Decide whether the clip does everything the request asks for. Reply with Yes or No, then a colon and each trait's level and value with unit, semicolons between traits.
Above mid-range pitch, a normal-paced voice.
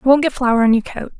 No: very high, 250 Hz; fast, 350 wpm